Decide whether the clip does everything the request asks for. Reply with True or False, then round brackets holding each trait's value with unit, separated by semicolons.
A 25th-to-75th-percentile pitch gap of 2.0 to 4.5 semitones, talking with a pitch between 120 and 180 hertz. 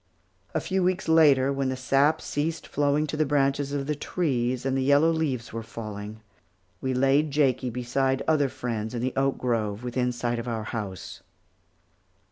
True (3.3 semitones; 135 Hz)